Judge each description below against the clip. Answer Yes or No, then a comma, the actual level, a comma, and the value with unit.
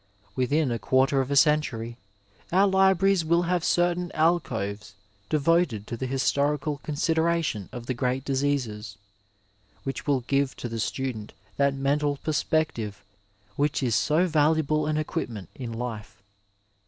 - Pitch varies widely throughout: No, average, 4.7 semitones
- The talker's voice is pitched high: No, medium, 140 Hz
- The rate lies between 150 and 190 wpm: No, average, 140 wpm